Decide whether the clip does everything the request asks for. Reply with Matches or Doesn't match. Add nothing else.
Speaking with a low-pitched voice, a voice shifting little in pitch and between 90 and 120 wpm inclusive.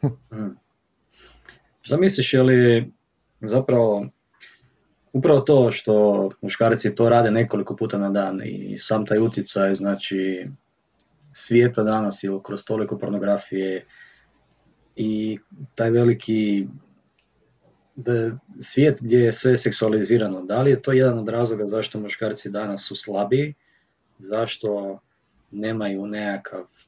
Doesn't match